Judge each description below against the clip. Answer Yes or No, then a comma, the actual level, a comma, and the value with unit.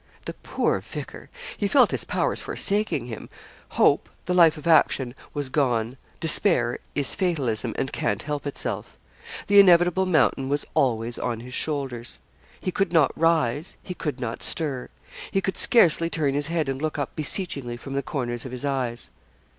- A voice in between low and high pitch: Yes, medium, 145 Hz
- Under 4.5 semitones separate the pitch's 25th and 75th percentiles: No, average, 5.0 semitones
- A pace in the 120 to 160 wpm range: No, average, 170 wpm